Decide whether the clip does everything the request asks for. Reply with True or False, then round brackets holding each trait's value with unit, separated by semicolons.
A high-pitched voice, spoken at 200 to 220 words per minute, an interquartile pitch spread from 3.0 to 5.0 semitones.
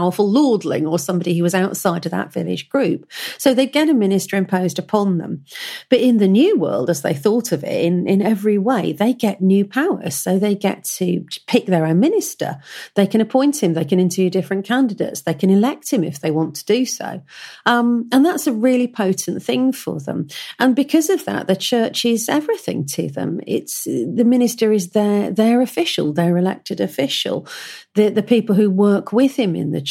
False (210 Hz; 205 wpm; 5.4 semitones)